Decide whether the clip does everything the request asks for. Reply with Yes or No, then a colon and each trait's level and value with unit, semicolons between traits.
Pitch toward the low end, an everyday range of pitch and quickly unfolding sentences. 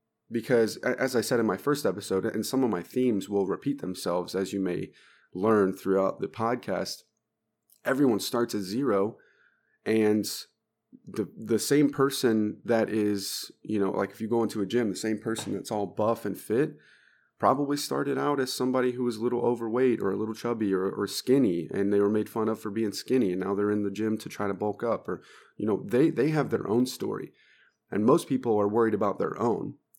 Yes: low, 110 Hz; average, 3.5 semitones; fast, 210 wpm